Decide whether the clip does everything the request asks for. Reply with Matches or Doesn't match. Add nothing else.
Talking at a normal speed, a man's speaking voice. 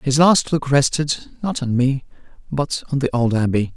Matches